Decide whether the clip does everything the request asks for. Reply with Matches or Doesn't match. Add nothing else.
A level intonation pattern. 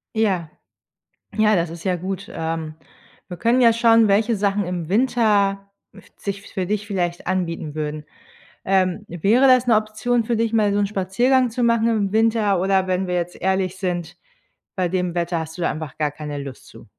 Doesn't match